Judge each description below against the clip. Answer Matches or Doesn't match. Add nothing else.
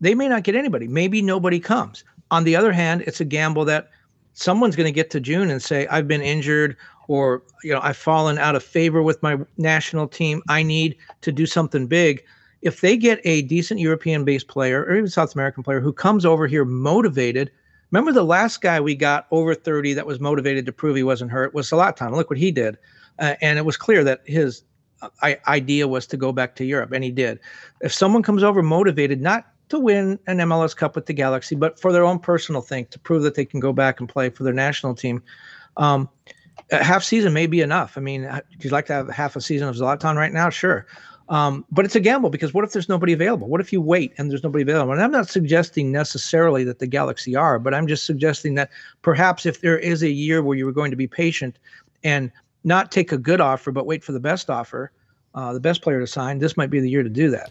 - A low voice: Doesn't match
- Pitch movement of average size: Matches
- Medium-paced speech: Doesn't match